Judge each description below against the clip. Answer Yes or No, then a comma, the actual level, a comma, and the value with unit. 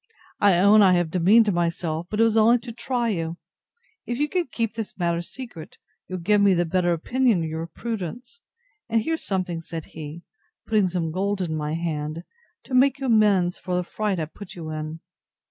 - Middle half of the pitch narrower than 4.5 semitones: No, average, 5.1 semitones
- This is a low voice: No, medium, 185 Hz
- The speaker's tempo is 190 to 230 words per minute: Yes, average, 195 wpm